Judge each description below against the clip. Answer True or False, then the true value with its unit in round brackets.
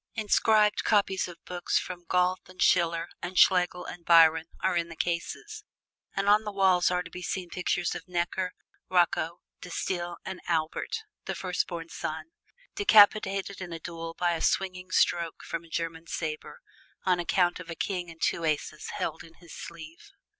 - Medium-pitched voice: True (175 Hz)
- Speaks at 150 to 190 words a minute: True (175 wpm)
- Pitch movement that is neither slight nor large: False (2.0 semitones)